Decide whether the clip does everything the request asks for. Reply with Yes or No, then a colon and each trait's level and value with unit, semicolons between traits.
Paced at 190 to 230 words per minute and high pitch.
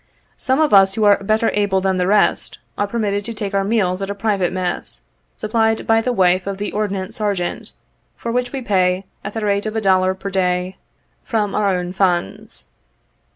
Yes: average, 200 wpm; high, 200 Hz